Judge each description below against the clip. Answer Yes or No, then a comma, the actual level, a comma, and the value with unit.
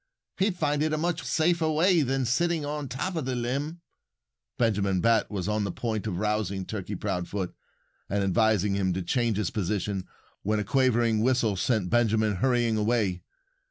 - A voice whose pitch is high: No, low, 115 Hz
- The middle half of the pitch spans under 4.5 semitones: No, average, 5.2 semitones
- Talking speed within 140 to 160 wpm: No, average, 170 wpm